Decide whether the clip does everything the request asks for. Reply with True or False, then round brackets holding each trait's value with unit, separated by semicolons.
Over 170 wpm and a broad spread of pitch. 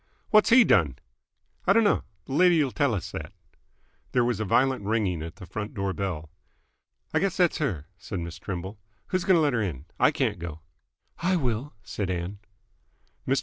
True (185 wpm; 8.5 semitones)